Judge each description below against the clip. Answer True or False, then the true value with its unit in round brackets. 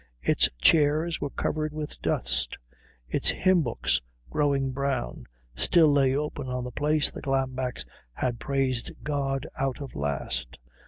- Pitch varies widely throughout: False (2.8 semitones)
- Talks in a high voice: False (135 Hz)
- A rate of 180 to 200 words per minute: False (140 wpm)